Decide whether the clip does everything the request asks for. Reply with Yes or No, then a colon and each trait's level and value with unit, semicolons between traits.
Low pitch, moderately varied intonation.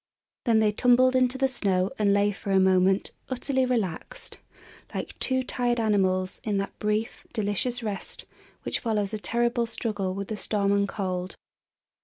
No: high, 210 Hz; average, 3.7 semitones